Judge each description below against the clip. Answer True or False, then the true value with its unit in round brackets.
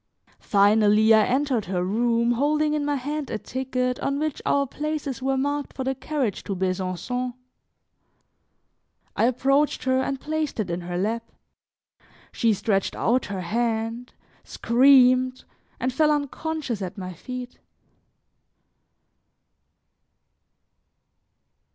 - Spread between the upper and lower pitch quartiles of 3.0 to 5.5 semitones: True (4.3 semitones)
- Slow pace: True (120 wpm)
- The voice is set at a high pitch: True (250 Hz)